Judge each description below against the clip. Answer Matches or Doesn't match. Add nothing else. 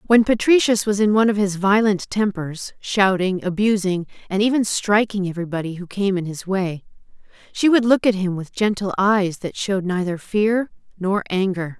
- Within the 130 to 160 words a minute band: Doesn't match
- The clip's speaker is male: Doesn't match